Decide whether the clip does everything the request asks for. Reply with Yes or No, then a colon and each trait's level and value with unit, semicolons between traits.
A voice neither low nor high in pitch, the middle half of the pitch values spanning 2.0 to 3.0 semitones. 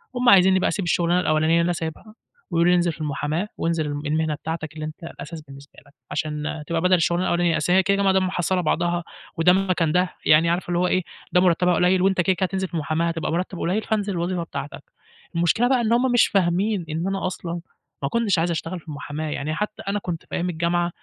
Yes: medium, 175 Hz; average, 2.7 semitones